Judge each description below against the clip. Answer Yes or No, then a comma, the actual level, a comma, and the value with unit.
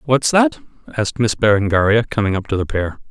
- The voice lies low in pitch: Yes, low, 105 Hz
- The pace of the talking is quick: No, average, 195 wpm